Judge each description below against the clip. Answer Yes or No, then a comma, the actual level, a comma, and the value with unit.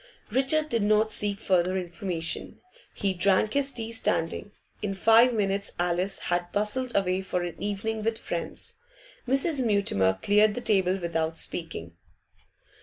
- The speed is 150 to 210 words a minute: No, average, 140 wpm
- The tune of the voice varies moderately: Yes, average, 3.9 semitones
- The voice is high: Yes, high, 200 Hz